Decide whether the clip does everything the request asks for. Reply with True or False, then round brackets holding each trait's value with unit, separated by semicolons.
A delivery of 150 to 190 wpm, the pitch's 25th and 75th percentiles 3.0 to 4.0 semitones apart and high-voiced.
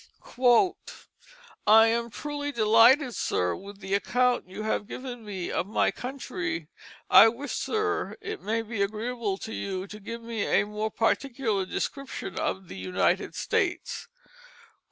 False (140 wpm; 3.7 semitones; 225 Hz)